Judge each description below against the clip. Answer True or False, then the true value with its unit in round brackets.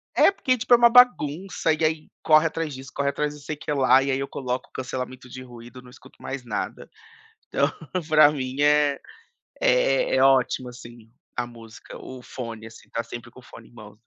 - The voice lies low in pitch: True (130 Hz)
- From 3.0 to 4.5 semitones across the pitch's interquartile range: True (3.3 semitones)